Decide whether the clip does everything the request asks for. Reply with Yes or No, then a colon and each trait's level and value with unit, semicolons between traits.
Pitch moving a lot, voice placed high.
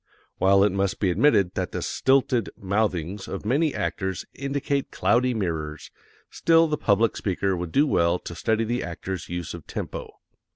No: wide, 6.2 semitones; low, 100 Hz